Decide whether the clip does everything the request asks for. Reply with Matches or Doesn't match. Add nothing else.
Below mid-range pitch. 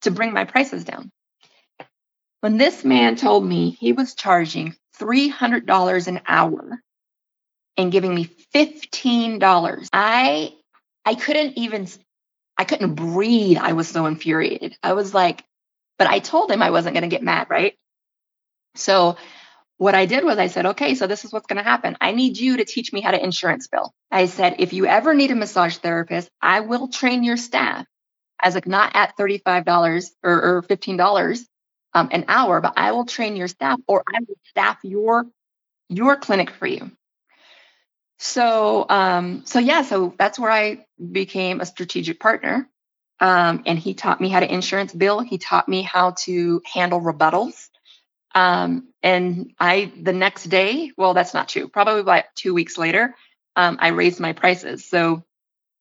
Doesn't match